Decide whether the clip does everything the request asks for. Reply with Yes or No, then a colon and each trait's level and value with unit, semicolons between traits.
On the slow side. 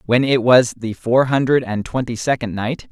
No: fast, 205 wpm